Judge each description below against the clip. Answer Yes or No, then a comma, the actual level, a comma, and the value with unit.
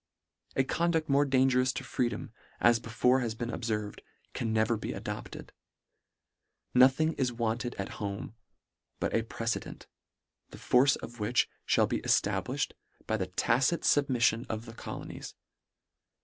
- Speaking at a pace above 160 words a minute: No, average, 150 wpm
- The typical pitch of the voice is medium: No, low, 120 Hz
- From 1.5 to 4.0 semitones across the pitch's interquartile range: Yes, average, 2.8 semitones